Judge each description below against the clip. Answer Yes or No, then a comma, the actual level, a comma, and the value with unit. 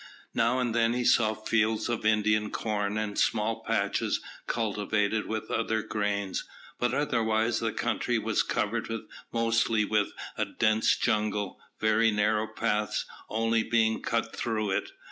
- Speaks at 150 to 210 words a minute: No, average, 140 wpm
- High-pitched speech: No, low, 110 Hz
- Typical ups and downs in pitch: No, narrow, 1.2 semitones